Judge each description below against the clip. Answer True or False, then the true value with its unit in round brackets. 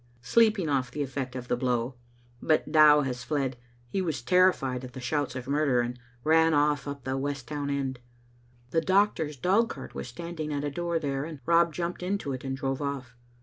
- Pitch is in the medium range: True (145 Hz)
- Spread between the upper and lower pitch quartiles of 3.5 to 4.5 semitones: True (3.8 semitones)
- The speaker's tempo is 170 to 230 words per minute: True (200 wpm)